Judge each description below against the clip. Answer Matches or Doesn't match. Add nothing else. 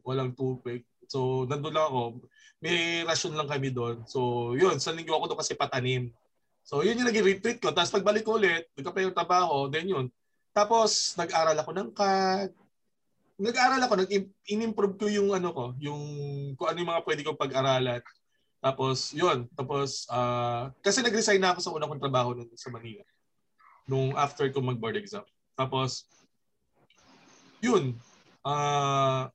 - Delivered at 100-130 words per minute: Doesn't match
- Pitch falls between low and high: Matches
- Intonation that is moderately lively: Doesn't match